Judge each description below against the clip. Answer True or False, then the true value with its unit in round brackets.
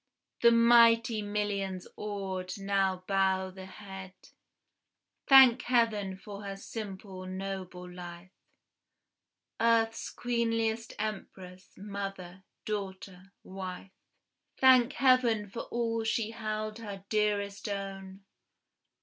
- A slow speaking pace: True (95 wpm)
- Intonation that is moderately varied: True (3.0 semitones)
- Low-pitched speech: False (200 Hz)